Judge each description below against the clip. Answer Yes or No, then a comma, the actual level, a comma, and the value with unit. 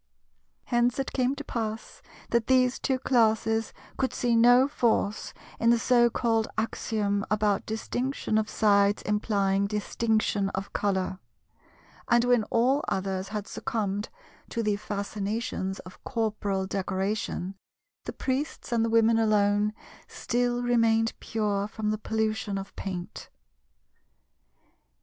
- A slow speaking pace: Yes, slow, 125 wpm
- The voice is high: Yes, high, 220 Hz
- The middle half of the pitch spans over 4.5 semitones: No, average, 2.7 semitones